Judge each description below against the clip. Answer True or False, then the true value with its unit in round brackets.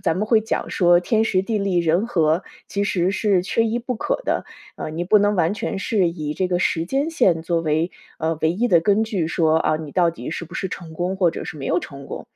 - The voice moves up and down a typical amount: True (4.1 semitones)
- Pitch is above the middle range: False (180 Hz)